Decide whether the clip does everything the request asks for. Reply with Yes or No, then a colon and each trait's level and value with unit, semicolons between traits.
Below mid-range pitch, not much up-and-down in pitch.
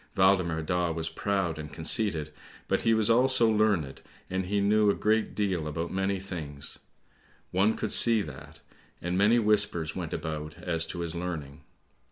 No: very low, 90 Hz; average, 4.6 semitones